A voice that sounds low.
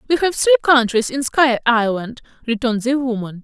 No: very high, 250 Hz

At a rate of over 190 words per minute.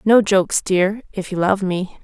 Yes: fast, 205 wpm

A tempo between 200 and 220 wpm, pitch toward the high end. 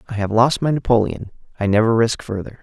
No: fast, 205 wpm; low, 115 Hz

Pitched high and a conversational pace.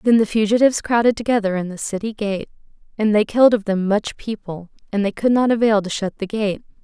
No: high, 210 Hz; fast, 220 wpm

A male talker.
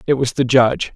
Yes: male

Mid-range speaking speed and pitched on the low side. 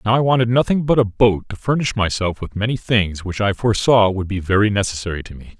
No: fast, 235 wpm; low, 105 Hz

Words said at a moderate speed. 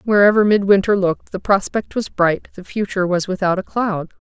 Yes: average, 185 wpm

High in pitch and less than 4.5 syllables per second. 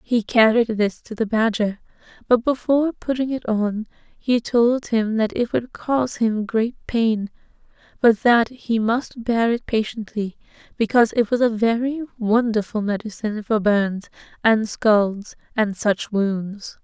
Yes: high, 225 Hz; 4.1 syllables/s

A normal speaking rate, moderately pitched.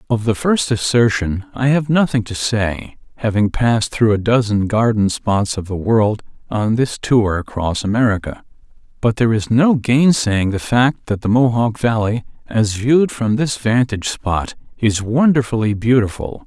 No: average, 160 wpm; low, 115 Hz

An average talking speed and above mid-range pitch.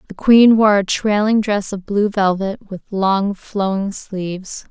Yes: average, 165 wpm; high, 200 Hz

